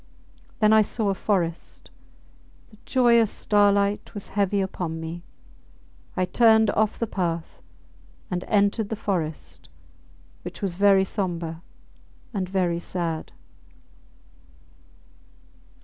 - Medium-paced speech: No, slow, 105 wpm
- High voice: Yes, high, 195 Hz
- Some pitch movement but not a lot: Yes, average, 3.4 semitones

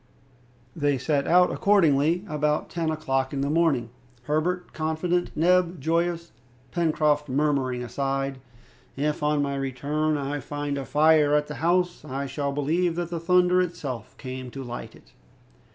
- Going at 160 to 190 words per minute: No, average, 150 wpm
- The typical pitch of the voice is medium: Yes, medium, 150 Hz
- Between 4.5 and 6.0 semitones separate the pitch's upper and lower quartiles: No, average, 3.4 semitones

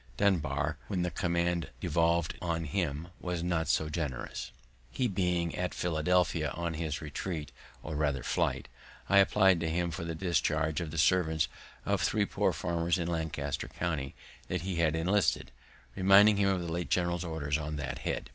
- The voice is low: Yes, very low, 85 Hz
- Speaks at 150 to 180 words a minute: Yes, average, 170 wpm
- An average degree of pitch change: No, narrow, 2.3 semitones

